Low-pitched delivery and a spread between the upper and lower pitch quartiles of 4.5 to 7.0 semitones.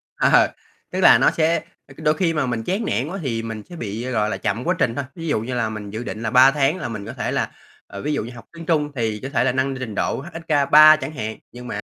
Yes: low, 130 Hz; average, 5.2 semitones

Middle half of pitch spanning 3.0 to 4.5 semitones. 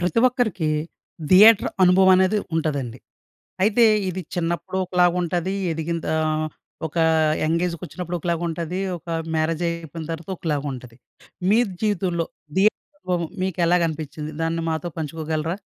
No: narrow, 2.4 semitones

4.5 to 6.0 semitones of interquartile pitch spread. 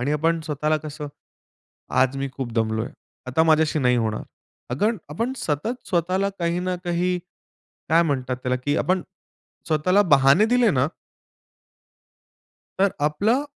Yes: average, 5.2 semitones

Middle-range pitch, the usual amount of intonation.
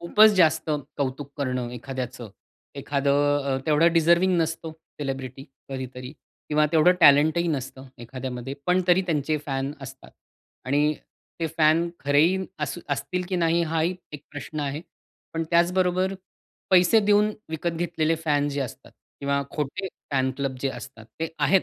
Yes: medium, 150 Hz; average, 4.0 semitones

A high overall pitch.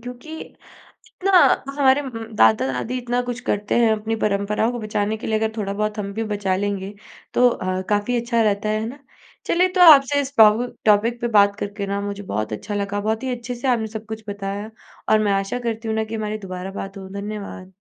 Yes: high, 215 Hz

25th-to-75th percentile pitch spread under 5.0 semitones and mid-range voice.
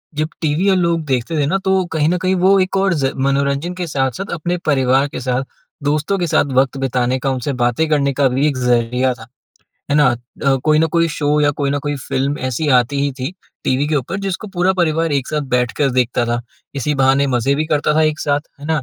Yes: average, 3.5 semitones; medium, 145 Hz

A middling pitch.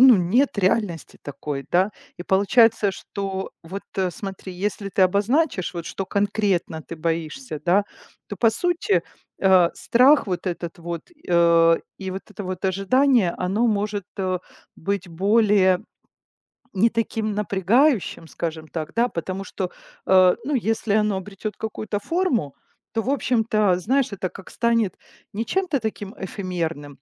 No: high, 195 Hz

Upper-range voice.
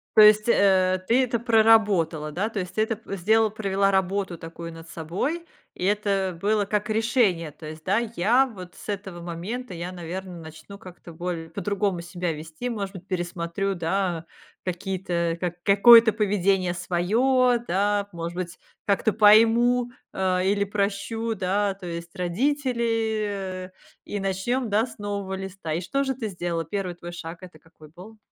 Yes: high, 195 Hz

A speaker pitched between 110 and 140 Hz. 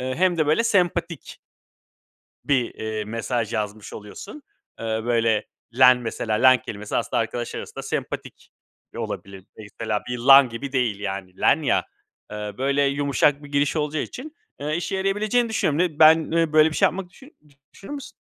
Yes: low, 135 Hz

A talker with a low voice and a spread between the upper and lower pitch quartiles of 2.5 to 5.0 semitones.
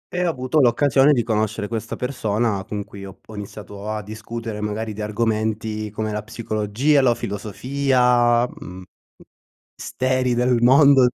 Yes: low, 115 Hz; average, 2.9 semitones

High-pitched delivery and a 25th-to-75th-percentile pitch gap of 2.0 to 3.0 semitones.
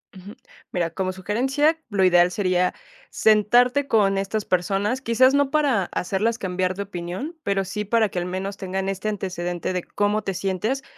No: high, 195 Hz; average, 3.4 semitones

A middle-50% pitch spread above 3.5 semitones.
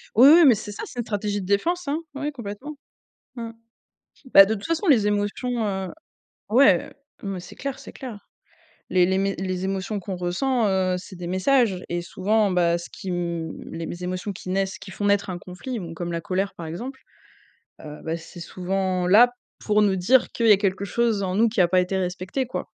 Yes: average, 3.9 semitones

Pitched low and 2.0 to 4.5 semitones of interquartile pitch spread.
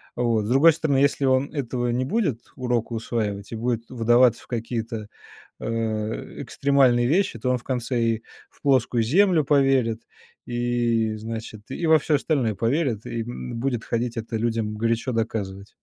Yes: low, 120 Hz; average, 2.8 semitones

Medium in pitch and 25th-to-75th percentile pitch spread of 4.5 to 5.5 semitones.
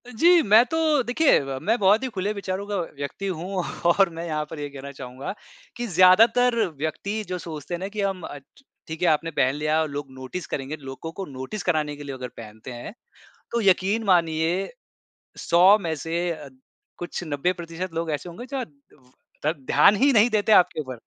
Yes: medium, 175 Hz; average, 5.2 semitones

